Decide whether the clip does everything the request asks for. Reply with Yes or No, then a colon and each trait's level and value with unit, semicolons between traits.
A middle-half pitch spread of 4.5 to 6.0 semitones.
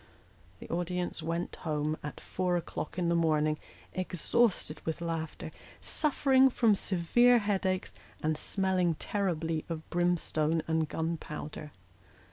No: average, 2.9 semitones